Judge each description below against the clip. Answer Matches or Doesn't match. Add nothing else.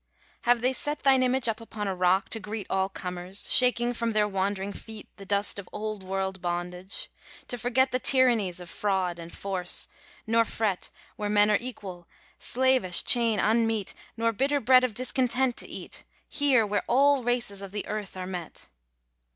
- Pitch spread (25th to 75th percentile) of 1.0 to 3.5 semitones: Doesn't match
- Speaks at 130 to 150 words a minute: Doesn't match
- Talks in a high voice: Matches